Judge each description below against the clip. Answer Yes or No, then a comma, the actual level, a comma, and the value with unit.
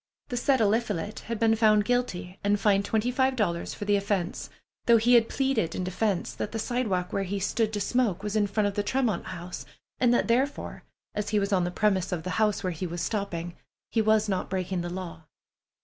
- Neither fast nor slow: No, fast, 220 wpm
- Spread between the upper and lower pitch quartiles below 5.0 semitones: Yes, average, 3.5 semitones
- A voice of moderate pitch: No, high, 205 Hz